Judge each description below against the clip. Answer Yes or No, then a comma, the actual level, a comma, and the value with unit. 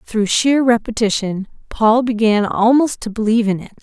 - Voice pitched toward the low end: No, high, 225 Hz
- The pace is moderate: Yes, average, 155 wpm